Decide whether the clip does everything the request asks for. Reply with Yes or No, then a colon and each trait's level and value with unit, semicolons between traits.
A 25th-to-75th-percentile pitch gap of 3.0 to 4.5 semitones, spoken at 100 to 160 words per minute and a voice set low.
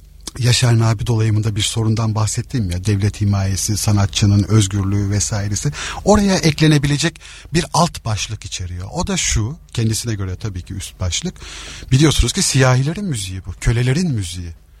No: average, 5.2 semitones; fast, 140 wpm; low, 110 Hz